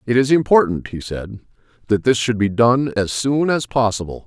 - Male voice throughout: Yes, male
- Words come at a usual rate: Yes, average, 195 wpm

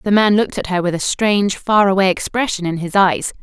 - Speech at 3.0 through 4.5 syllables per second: No, 5.7 syllables/s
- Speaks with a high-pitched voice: Yes, high, 195 Hz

